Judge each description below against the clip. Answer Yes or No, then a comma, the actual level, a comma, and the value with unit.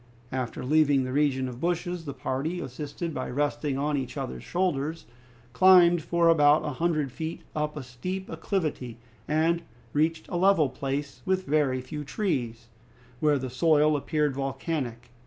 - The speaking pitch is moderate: Yes, medium, 150 Hz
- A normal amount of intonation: Yes, average, 3.8 semitones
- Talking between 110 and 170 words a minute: Yes, average, 155 wpm